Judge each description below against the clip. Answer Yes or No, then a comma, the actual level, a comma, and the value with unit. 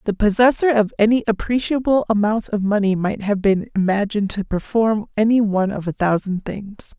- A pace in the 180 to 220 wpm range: No, average, 170 wpm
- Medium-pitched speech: No, high, 210 Hz